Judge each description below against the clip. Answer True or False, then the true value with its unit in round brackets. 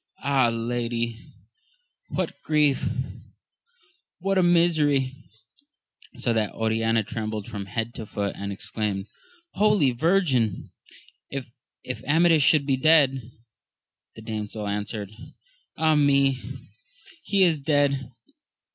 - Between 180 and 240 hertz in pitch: False (130 Hz)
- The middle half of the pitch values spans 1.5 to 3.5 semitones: False (5.6 semitones)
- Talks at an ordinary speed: False (110 wpm)